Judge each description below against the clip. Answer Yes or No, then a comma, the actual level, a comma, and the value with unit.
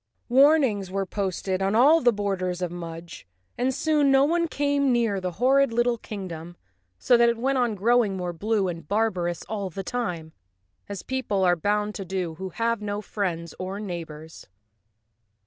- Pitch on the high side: Yes, high, 205 Hz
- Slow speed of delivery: No, average, 170 wpm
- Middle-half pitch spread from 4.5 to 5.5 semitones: Yes, average, 5.1 semitones